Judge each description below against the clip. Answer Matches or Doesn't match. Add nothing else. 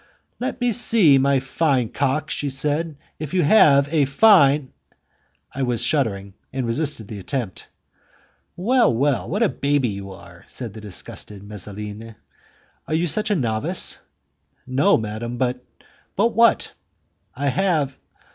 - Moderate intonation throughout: Doesn't match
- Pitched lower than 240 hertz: Matches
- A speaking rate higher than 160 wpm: Doesn't match